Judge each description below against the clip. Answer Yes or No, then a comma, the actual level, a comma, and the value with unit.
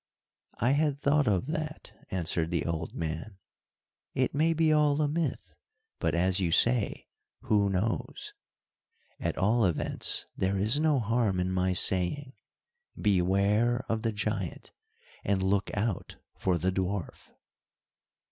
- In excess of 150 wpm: No, slow, 135 wpm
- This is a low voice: Yes, low, 105 Hz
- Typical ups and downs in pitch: No, wide, 5.8 semitones